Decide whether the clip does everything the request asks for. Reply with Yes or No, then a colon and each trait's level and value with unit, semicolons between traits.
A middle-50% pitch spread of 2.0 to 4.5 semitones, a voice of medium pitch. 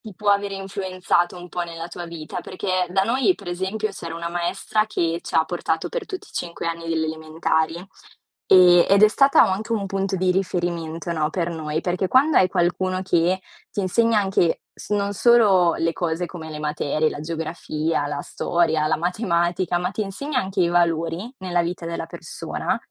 Yes: average, 2.7 semitones; medium, 175 Hz